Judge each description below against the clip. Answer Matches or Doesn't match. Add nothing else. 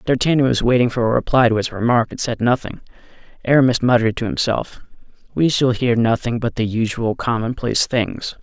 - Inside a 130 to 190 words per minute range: Matches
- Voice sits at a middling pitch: Doesn't match